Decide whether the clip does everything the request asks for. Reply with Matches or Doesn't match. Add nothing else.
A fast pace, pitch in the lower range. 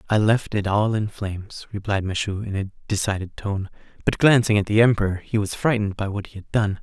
Matches